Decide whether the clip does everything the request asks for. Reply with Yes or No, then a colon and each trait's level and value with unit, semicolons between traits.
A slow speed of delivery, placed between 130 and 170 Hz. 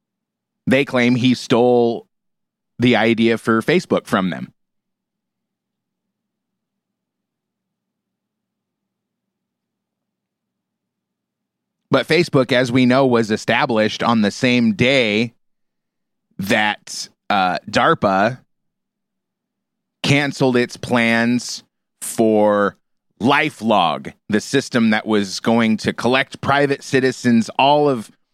Yes: slow, 85 wpm; medium, 140 Hz